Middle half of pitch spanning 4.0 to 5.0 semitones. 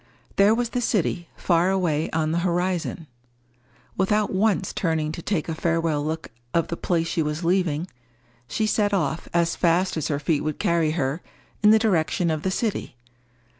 No: average, 3.2 semitones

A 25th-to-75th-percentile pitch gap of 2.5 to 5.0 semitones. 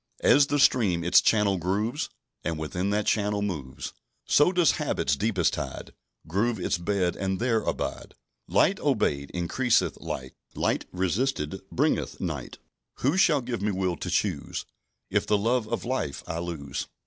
No: wide, 5.6 semitones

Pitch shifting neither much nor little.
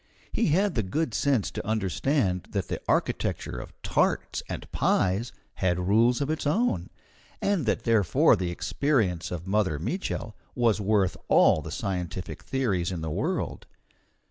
No: wide, 6.8 semitones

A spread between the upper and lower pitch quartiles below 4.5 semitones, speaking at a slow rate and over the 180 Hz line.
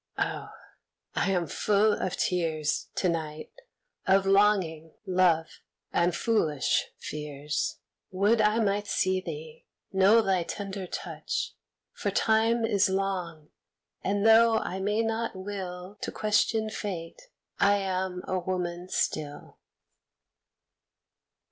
Yes: average, 3.3 semitones; slow, 115 wpm; high, 190 Hz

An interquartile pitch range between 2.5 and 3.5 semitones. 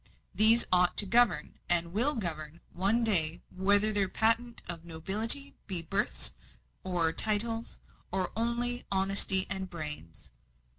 No: average, 4.8 semitones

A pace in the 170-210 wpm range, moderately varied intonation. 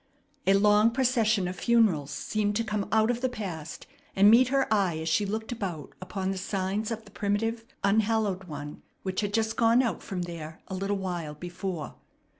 Yes: average, 190 wpm; average, 3.4 semitones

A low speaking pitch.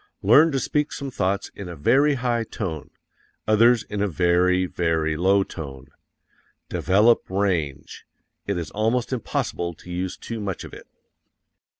Yes: very low, 95 Hz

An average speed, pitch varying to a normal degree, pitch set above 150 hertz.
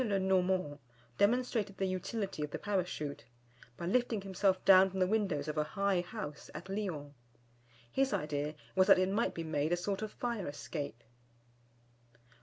Yes: average, 165 wpm; average, 4.7 semitones; medium, 185 Hz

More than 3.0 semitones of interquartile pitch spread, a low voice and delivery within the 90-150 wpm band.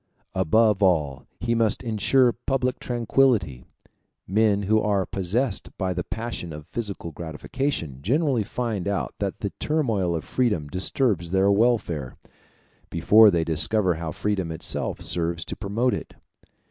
Yes: wide, 5.4 semitones; low, 100 Hz; slow, 135 wpm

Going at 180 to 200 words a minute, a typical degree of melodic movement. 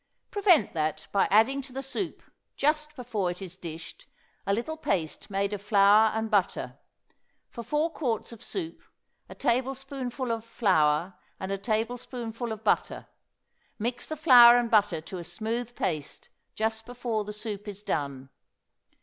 No: average, 155 wpm; average, 4.1 semitones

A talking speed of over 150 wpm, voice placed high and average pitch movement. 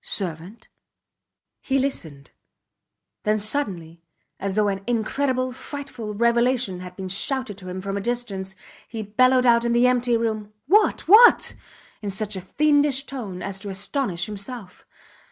No: average, 145 wpm; high, 220 Hz; average, 4.7 semitones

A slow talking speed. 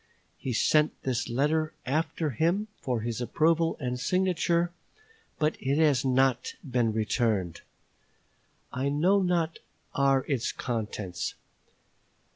Yes: slow, 115 wpm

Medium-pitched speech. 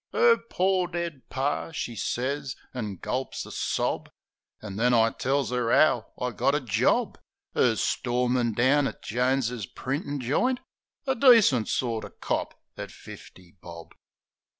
No: low, 130 Hz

